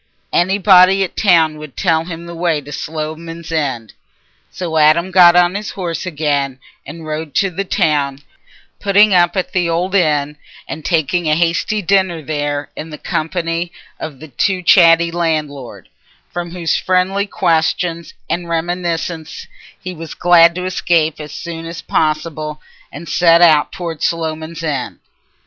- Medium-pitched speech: Yes, medium, 165 Hz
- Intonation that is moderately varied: No, narrow, 2.3 semitones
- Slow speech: No, average, 155 wpm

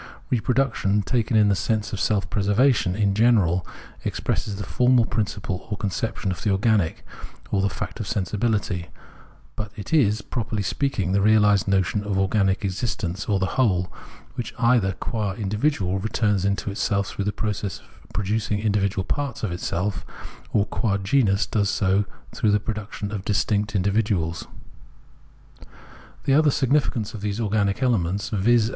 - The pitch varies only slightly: Yes, narrow, 2.3 semitones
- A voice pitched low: Yes, low, 105 Hz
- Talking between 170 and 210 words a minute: No, average, 160 wpm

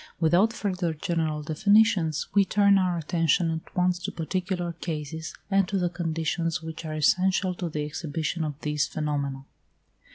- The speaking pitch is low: No, medium, 165 Hz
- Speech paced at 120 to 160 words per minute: Yes, average, 155 wpm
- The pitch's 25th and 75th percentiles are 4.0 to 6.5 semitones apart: No, average, 2.8 semitones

